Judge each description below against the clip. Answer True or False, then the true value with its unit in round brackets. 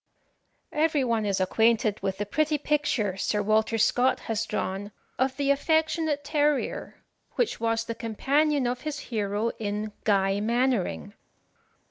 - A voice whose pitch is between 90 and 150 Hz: False (230 Hz)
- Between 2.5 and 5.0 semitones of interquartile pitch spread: False (5.6 semitones)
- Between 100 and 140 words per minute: True (135 wpm)